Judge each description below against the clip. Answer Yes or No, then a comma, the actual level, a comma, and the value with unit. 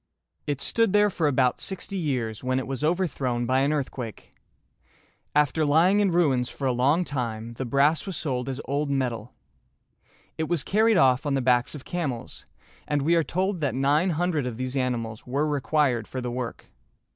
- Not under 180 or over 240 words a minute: Yes, average, 185 wpm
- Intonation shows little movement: No, average, 4.2 semitones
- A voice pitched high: No, medium, 140 Hz